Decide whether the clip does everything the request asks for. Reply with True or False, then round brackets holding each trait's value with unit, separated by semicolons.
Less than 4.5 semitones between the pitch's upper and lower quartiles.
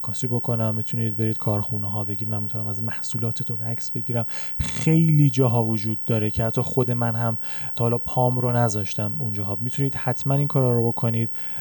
True (2.4 semitones)